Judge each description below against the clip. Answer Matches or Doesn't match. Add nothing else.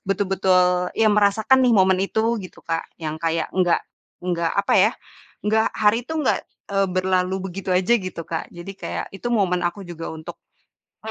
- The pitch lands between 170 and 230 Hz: Matches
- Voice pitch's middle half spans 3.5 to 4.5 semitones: Doesn't match